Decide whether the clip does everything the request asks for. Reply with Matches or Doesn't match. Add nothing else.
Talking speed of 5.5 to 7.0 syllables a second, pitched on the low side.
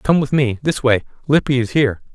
Matches